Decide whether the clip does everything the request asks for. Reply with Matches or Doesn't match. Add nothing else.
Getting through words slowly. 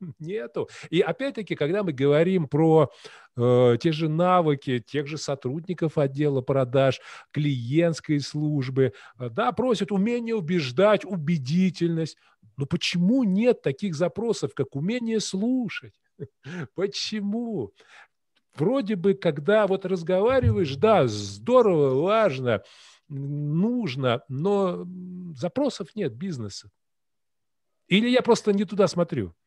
Matches